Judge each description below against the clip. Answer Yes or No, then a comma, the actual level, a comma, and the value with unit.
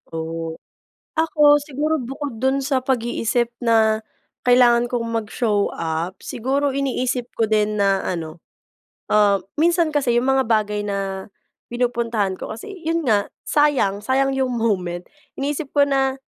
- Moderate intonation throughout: Yes, average, 4.6 semitones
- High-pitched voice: Yes, high, 240 Hz